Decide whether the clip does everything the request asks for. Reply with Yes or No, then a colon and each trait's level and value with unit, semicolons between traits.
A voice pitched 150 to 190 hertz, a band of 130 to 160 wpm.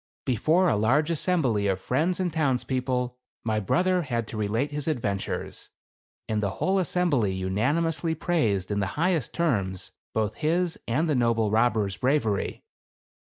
No: low, 125 Hz; average, 155 wpm